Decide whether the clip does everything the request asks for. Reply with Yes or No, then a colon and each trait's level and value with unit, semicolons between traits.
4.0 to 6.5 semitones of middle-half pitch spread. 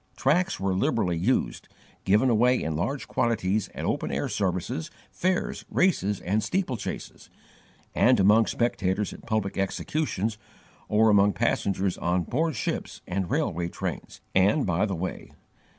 Yes: average, 4.8 semitones